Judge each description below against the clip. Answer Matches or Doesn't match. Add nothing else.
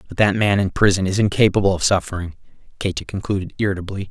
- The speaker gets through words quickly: Doesn't match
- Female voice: Doesn't match